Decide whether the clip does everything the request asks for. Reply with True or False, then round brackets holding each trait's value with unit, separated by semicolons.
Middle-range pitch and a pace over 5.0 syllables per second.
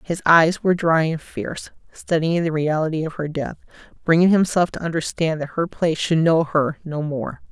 True (160 Hz; 5.2 syllables/s)